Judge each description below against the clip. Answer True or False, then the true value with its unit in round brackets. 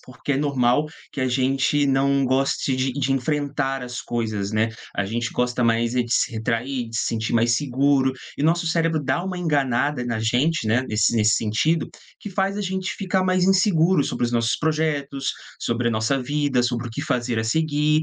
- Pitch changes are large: False (4.2 semitones)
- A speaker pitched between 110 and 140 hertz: True (135 Hz)